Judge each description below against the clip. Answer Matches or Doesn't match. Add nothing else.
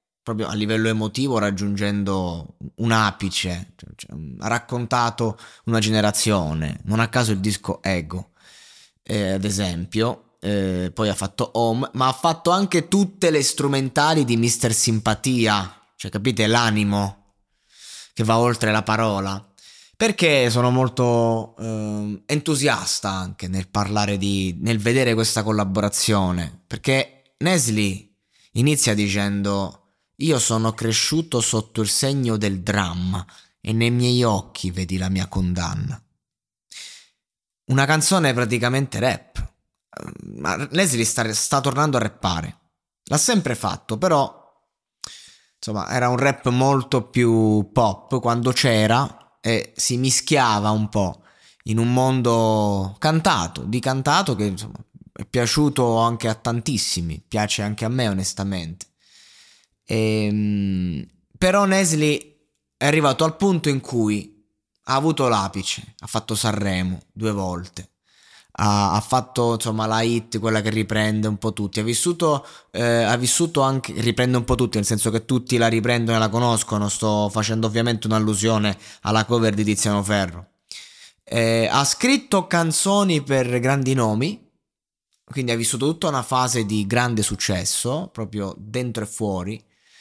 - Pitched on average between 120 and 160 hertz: Doesn't match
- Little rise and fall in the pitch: Doesn't match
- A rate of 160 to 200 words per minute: Doesn't match